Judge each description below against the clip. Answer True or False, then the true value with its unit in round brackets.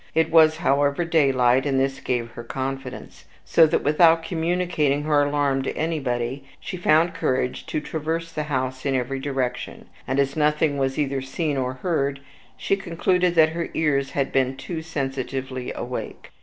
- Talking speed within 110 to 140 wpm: False (165 wpm)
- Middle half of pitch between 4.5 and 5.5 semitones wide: False (3.3 semitones)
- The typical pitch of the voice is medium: True (145 Hz)